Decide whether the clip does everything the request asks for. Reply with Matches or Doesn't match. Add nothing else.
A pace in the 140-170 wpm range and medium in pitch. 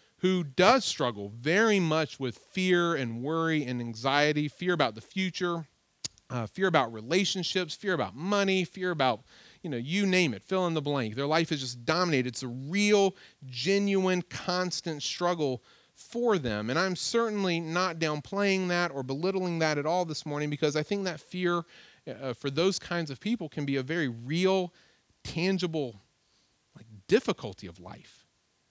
Matches